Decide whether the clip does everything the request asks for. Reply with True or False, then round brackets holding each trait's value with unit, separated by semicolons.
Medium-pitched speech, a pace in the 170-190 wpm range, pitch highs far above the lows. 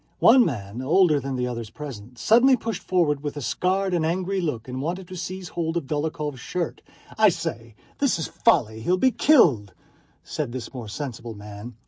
True (150 Hz; 185 wpm; 7.3 semitones)